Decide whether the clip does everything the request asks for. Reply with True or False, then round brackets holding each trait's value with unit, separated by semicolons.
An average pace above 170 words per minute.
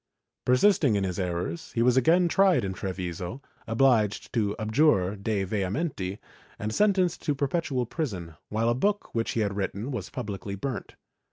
False (160 wpm)